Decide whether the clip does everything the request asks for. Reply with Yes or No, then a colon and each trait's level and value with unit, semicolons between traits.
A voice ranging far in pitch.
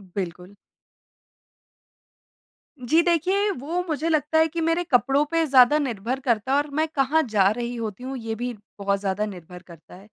Yes: wide, 7.2 semitones